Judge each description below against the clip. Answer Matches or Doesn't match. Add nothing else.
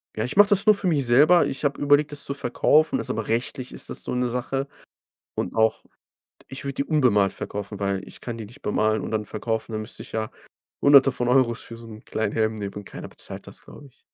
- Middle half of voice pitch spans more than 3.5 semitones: Matches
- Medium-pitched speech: Doesn't match